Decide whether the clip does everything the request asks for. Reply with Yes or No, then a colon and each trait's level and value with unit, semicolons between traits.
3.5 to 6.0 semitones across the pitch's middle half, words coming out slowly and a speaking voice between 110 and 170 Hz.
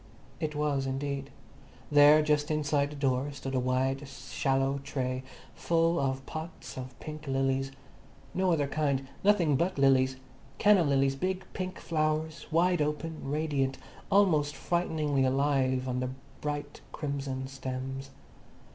No: narrow, 2.5 semitones; slow, 125 wpm; medium, 140 Hz